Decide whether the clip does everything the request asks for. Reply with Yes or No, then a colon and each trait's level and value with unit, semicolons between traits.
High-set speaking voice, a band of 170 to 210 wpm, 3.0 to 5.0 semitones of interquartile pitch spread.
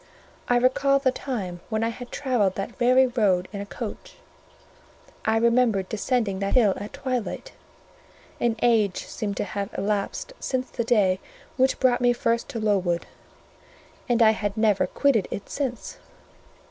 No: high, 225 Hz; average, 155 wpm; average, 3.8 semitones